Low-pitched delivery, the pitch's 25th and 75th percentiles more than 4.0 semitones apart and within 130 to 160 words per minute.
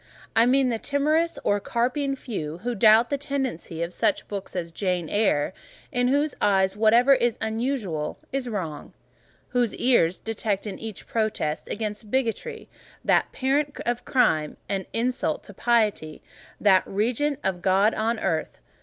No: high, 225 Hz; average, 5.0 semitones; average, 145 wpm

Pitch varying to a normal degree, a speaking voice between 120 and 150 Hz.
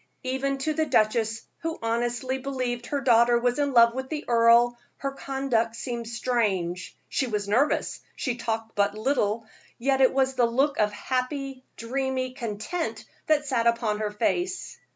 No: average, 3.0 semitones; high, 245 Hz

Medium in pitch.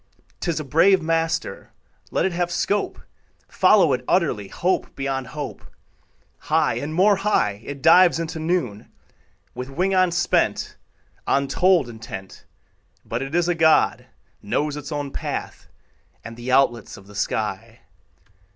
Yes: medium, 155 Hz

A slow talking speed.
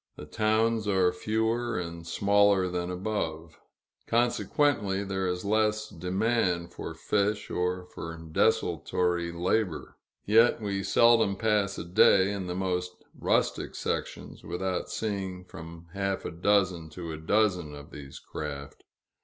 Yes: slow, 130 wpm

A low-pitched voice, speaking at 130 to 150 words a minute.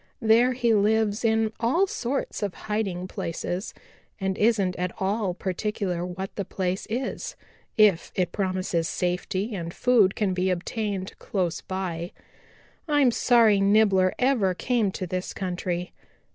No: high, 195 Hz; slow, 135 wpm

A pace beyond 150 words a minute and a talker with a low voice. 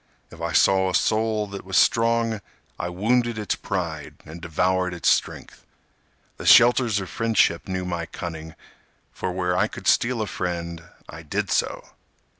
Yes: average, 160 wpm; very low, 95 Hz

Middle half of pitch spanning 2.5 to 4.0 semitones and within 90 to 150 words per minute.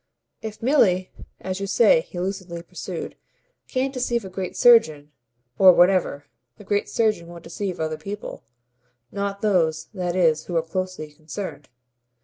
Yes: average, 3.4 semitones; average, 145 wpm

